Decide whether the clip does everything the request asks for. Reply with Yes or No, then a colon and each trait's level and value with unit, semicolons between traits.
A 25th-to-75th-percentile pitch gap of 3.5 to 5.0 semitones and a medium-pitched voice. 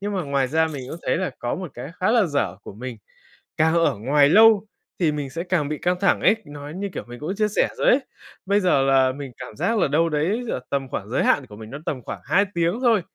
No: wide, 5.6 semitones; medium, 155 Hz